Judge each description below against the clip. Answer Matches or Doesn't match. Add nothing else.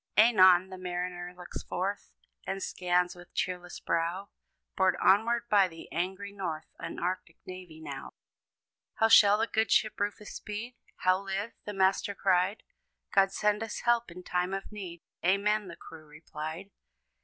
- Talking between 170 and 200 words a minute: Doesn't match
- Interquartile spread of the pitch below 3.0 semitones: Matches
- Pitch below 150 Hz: Doesn't match